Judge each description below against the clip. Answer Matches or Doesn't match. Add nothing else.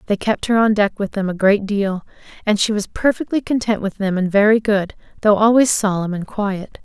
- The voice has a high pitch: Matches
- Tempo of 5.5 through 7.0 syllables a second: Doesn't match